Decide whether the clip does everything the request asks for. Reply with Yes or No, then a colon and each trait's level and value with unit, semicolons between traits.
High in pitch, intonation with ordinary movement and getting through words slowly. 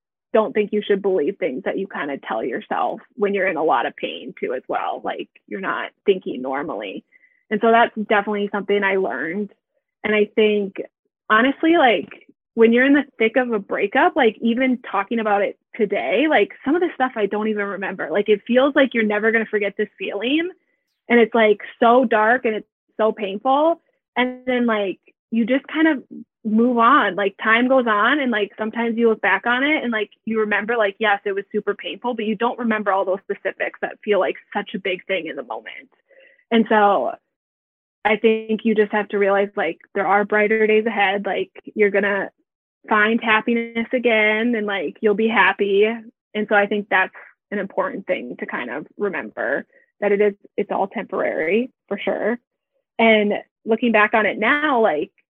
No: high, 220 Hz; average, 3.0 semitones; average, 200 wpm